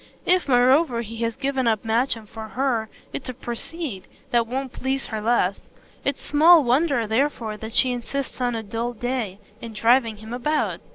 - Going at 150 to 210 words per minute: Yes, average, 175 wpm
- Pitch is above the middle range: Yes, high, 240 Hz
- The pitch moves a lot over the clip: No, average, 3.1 semitones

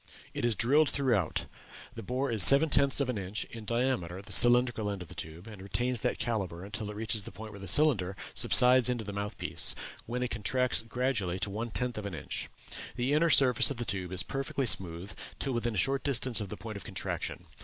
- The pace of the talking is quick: Yes, fast, 230 wpm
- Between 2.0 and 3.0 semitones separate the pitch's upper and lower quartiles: No, average, 4.3 semitones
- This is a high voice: No, low, 115 Hz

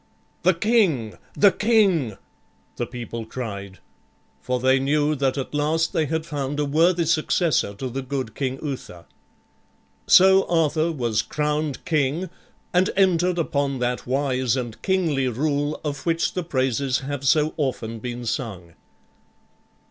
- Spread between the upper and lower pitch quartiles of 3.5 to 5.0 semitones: Yes, average, 4.3 semitones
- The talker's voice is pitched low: No, medium, 145 Hz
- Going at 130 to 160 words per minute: Yes, average, 140 wpm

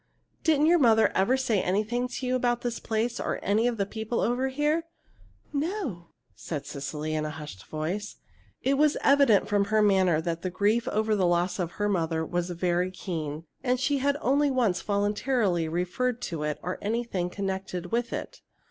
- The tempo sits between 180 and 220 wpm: Yes, average, 185 wpm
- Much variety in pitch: Yes, wide, 5.9 semitones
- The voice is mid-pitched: No, high, 205 Hz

